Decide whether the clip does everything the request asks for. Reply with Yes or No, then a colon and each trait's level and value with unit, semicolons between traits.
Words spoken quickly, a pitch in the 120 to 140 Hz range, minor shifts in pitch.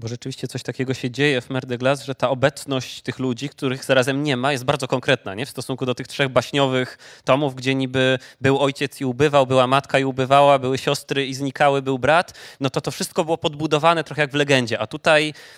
Yes: fast, 220 wpm; low, 135 Hz; narrow, 1.7 semitones